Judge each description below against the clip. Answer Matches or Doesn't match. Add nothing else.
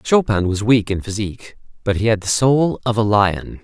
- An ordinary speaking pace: Doesn't match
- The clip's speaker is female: Doesn't match